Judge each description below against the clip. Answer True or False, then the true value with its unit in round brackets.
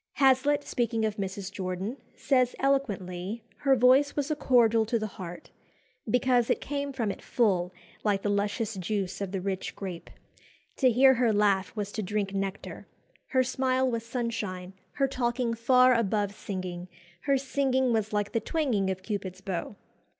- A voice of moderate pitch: False (220 Hz)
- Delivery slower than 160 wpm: False (165 wpm)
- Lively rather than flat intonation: False (4.6 semitones)